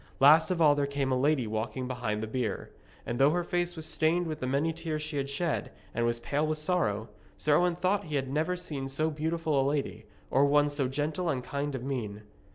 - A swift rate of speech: Yes, fast, 230 wpm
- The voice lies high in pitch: No, medium, 145 Hz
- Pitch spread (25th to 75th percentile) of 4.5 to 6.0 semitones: No, average, 3.5 semitones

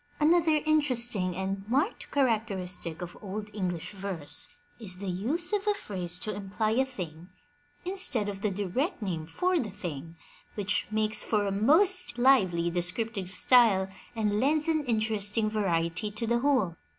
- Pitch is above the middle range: Yes, high, 210 Hz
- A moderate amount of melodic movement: No, wide, 5.8 semitones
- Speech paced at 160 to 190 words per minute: No, average, 150 wpm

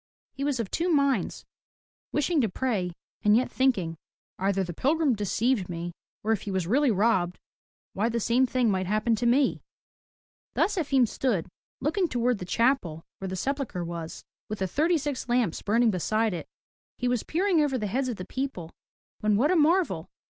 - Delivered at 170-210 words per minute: Yes, average, 185 wpm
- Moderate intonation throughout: No, wide, 6.2 semitones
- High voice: Yes, high, 235 Hz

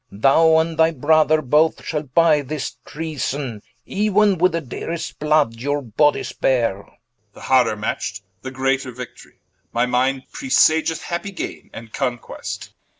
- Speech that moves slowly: No, average, 145 wpm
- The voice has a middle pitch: Yes, medium, 145 Hz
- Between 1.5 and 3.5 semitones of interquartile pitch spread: No, average, 4.2 semitones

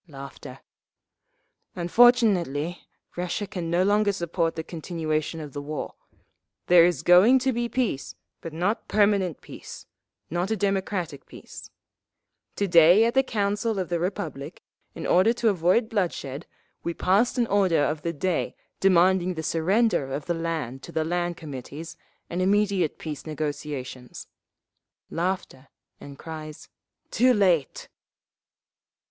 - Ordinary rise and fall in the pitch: Yes, average, 4.3 semitones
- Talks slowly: Yes, slow, 130 wpm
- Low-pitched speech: No, medium, 175 Hz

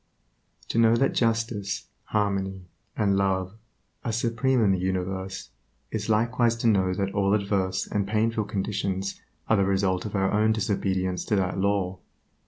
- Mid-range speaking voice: No, low, 100 Hz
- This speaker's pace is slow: No, average, 155 wpm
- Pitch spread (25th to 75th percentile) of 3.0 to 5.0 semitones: No, narrow, 2.5 semitones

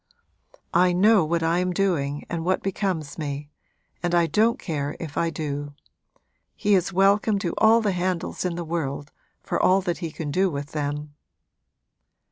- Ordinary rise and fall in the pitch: Yes, average, 4.1 semitones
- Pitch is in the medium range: Yes, medium, 170 Hz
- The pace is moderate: Yes, average, 170 wpm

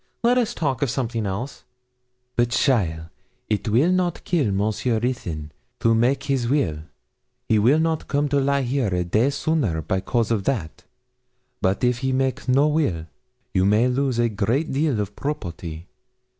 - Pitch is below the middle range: Yes, low, 120 Hz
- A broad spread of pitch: Yes, wide, 5.7 semitones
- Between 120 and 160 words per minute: No, average, 170 wpm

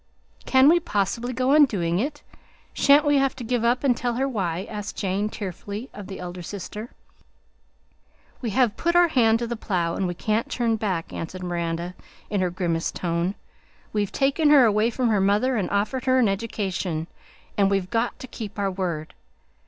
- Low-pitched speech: No, high, 210 Hz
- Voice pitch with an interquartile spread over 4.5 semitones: Yes, average, 5.2 semitones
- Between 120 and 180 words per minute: No, average, 190 wpm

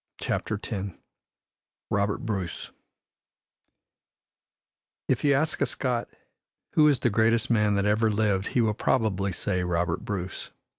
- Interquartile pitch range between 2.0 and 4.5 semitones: Yes, average, 2.8 semitones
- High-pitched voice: No, low, 105 Hz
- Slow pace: Yes, slow, 130 wpm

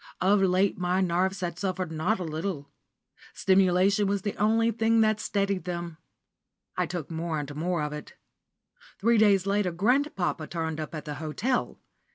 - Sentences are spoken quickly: No, average, 165 wpm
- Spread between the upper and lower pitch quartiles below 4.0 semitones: Yes, average, 3.5 semitones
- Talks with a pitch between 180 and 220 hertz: Yes, medium, 185 Hz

